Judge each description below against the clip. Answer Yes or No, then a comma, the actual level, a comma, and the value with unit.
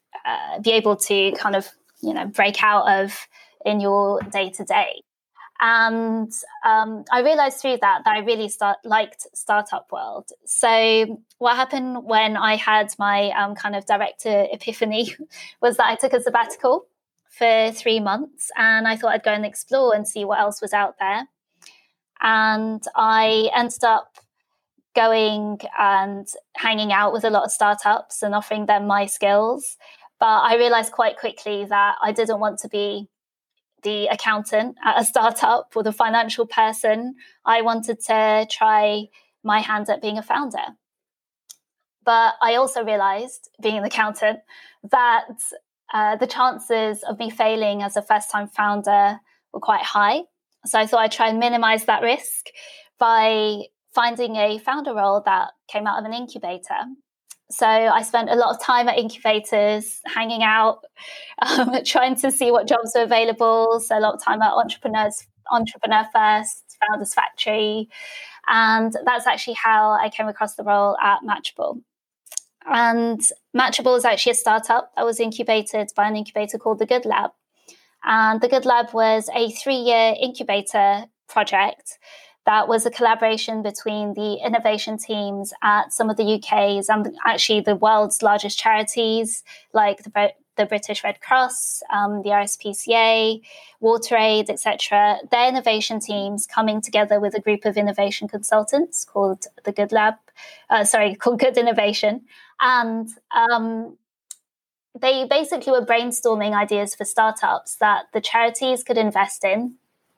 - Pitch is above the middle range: Yes, high, 220 Hz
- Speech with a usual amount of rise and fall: No, narrow, 2.2 semitones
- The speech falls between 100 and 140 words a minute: No, average, 155 wpm